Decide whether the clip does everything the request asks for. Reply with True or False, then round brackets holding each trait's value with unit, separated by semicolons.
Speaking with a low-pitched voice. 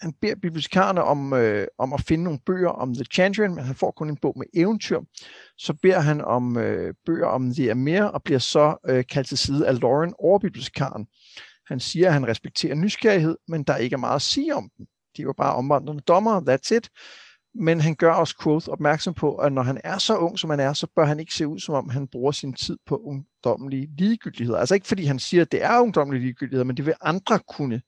False (155 Hz)